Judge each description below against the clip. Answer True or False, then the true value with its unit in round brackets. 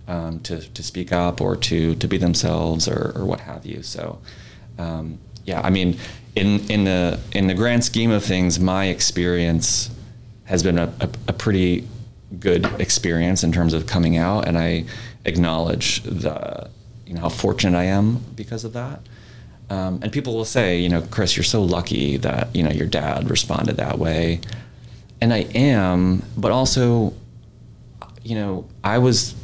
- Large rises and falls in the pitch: False (4.7 semitones)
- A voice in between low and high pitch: False (100 Hz)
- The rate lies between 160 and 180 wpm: True (175 wpm)